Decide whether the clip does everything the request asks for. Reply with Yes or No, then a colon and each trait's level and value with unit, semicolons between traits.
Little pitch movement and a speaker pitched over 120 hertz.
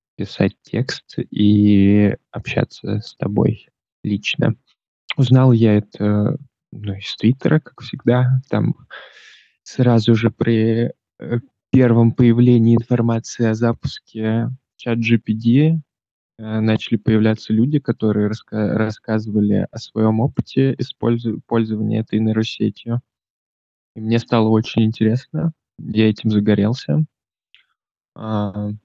No: narrow, 2.0 semitones; low, 115 Hz